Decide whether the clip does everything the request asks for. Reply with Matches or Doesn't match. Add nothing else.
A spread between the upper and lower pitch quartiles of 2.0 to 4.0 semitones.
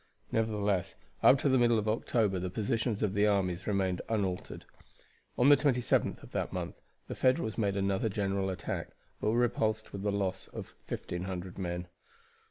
Matches